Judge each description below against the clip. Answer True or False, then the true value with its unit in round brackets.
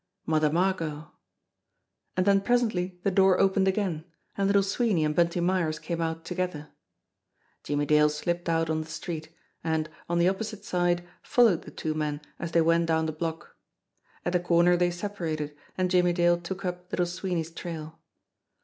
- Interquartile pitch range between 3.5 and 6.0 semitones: False (2.4 semitones)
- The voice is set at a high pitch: False (175 Hz)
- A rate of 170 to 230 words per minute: True (175 wpm)